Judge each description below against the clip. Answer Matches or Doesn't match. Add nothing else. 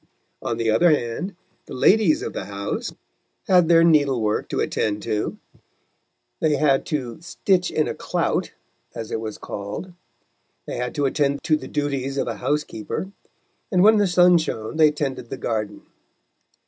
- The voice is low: Doesn't match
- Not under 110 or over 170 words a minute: Matches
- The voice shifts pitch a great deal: Matches